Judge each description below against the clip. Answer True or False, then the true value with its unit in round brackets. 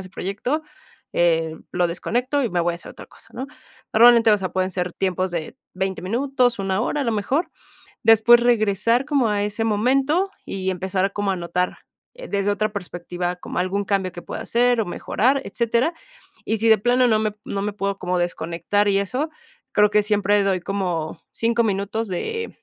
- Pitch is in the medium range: False (205 Hz)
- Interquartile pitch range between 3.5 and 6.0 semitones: True (4.2 semitones)